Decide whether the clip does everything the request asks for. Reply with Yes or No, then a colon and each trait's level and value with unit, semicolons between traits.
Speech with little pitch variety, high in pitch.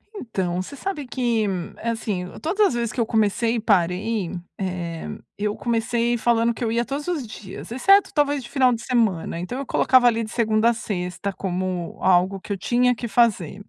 No: average, 4.1 semitones; high, 230 Hz